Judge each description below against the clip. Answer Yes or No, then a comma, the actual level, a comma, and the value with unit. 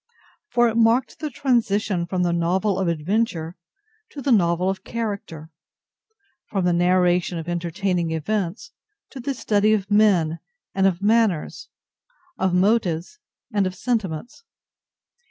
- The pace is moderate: No, slow, 130 wpm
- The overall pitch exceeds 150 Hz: Yes, high, 190 Hz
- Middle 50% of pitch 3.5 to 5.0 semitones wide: Yes, average, 4.6 semitones